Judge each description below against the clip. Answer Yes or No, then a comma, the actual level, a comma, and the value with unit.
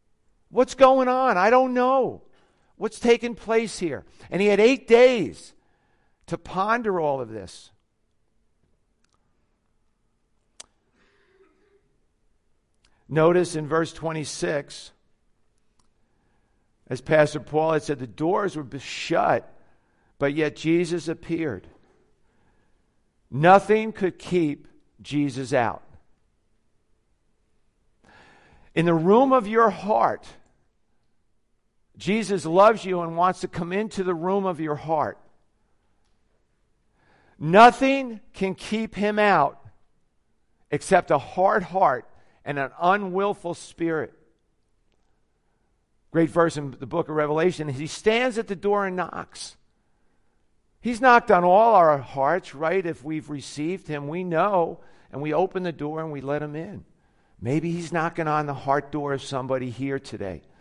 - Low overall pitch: No, medium, 160 Hz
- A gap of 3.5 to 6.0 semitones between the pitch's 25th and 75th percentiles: No, wide, 6.7 semitones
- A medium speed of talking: No, slow, 120 wpm